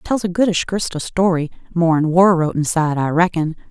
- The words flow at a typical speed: Yes, average, 195 wpm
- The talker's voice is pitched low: No, medium, 170 Hz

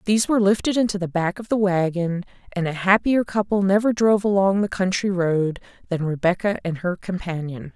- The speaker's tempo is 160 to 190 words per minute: Yes, average, 185 wpm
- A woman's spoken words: Yes, female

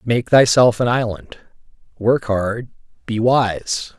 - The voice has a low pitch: Yes, low, 115 Hz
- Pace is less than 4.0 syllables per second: Yes, 3.3 syllables/s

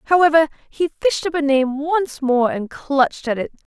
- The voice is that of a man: No, female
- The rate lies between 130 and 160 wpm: No, average, 190 wpm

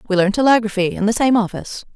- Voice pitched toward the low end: No, high, 215 Hz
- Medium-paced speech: No, fast, 215 wpm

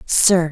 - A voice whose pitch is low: No, medium, 170 Hz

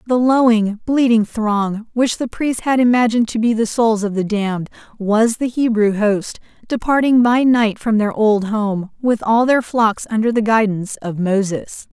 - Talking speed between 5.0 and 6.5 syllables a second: No, 4.5 syllables/s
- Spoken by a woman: Yes, female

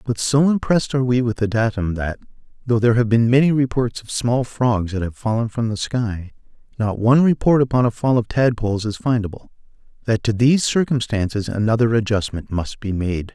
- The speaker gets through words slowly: No, average, 195 wpm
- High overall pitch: No, low, 115 Hz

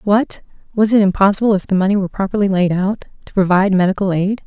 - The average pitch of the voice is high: Yes, high, 195 Hz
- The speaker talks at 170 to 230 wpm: Yes, average, 200 wpm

